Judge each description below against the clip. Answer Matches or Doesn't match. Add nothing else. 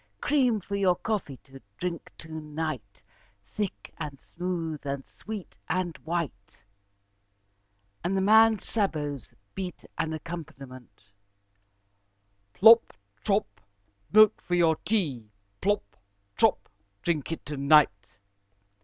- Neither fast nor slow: Doesn't match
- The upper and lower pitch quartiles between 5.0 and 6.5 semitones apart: Matches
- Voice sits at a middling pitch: Matches